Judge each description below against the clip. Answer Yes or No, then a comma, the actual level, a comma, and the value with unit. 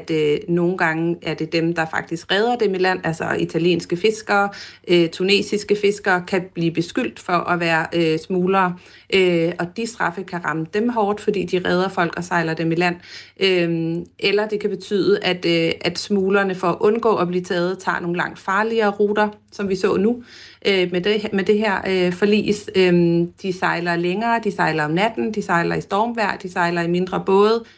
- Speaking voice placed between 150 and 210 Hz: Yes, medium, 185 Hz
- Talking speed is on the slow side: No, average, 200 wpm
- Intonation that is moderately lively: Yes, average, 3.0 semitones